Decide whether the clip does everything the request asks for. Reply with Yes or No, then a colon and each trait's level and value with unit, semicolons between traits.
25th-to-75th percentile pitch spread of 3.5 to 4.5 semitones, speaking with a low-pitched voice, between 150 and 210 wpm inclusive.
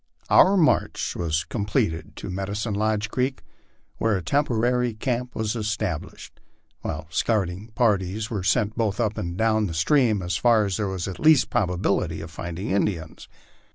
Yes: average, 4.1 semitones; low, 105 Hz; average, 155 wpm